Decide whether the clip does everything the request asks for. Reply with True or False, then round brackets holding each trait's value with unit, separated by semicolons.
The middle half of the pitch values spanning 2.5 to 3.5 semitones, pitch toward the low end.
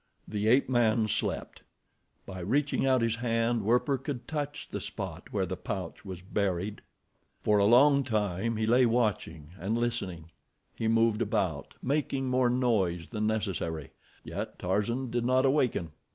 False (4.1 semitones; 115 Hz)